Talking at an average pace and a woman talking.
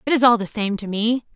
No: fast, 310 wpm; female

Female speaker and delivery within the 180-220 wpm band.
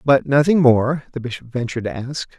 No: male; average, 200 wpm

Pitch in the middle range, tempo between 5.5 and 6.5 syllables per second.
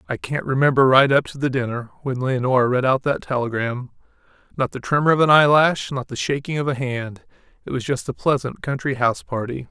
No: low, 130 Hz; 5.8 syllables/s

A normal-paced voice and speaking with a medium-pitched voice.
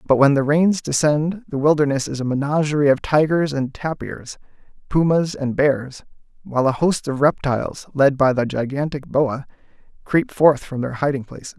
Yes: average, 170 wpm; medium, 145 Hz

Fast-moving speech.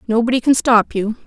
No: average, 190 wpm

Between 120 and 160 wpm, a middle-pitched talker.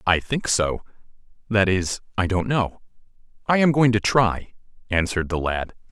No: average, 140 wpm; low, 100 Hz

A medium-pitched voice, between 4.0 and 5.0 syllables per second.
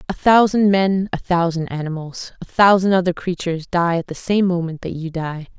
No: medium, 175 Hz; 5.2 syllables/s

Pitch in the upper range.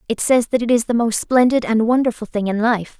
Yes: high, 230 Hz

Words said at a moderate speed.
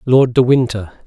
Yes: average, 170 wpm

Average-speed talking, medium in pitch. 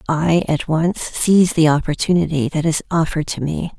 Yes: average, 175 wpm; medium, 160 Hz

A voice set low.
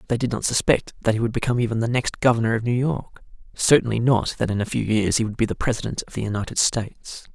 Yes: low, 115 Hz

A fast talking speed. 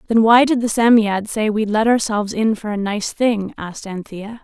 Yes: fast, 215 wpm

